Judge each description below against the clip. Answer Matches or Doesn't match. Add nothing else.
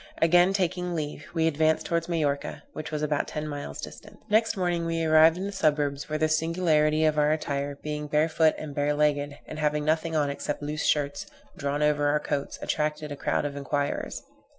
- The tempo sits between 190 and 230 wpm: Matches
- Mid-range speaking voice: Matches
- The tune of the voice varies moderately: Doesn't match